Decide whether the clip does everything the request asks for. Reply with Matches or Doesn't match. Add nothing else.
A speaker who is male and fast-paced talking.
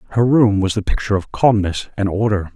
Matches